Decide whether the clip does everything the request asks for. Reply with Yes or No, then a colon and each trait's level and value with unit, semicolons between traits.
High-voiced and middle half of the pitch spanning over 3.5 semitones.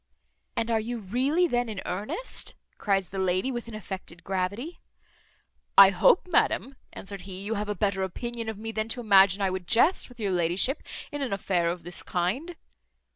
Yes: high, 205 Hz; average, 4.1 semitones